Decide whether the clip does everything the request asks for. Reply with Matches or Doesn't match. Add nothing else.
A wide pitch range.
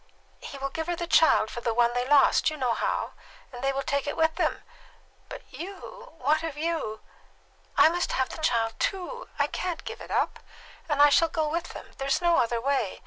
Doesn't match